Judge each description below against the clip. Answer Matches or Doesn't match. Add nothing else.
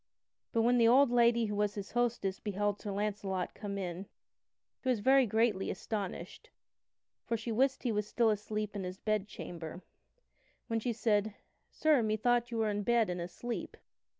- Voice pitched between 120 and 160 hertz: Doesn't match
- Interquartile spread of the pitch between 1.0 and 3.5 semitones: Matches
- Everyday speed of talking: Matches